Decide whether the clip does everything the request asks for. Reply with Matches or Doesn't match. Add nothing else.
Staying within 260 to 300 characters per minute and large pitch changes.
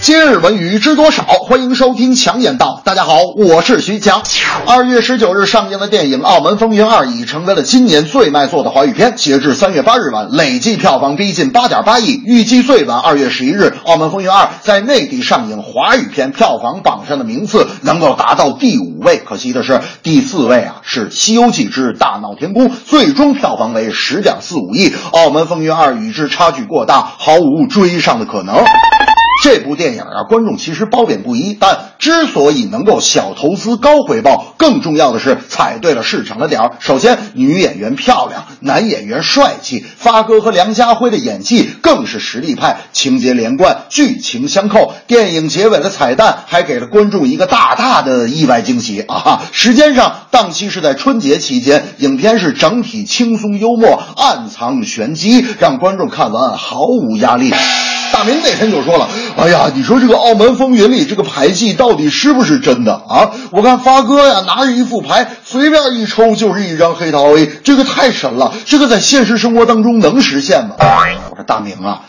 Doesn't match